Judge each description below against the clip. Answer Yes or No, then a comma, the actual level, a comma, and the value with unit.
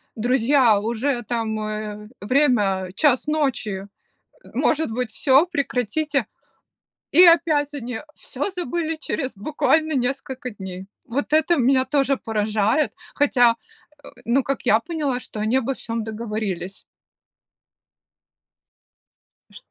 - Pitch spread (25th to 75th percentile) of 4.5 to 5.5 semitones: Yes, average, 4.9 semitones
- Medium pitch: No, very high, 250 Hz